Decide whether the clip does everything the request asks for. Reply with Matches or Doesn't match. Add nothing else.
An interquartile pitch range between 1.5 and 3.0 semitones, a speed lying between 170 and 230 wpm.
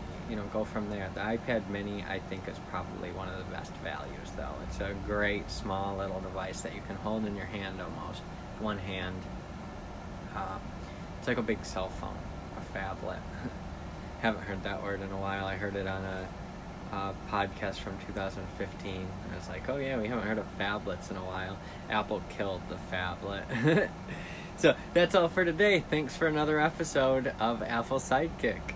Matches